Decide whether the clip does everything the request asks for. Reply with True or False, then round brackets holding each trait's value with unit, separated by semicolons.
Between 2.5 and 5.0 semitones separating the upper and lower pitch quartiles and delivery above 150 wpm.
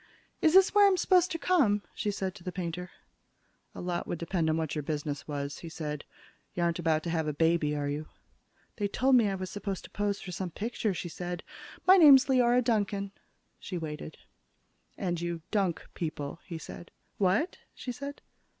False (5.6 semitones; 195 wpm)